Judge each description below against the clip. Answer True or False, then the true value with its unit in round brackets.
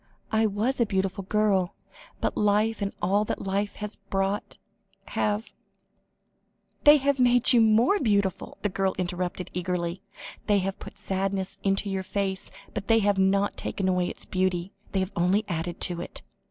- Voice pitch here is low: False (195 Hz)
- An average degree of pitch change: False (2.1 semitones)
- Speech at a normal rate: True (165 wpm)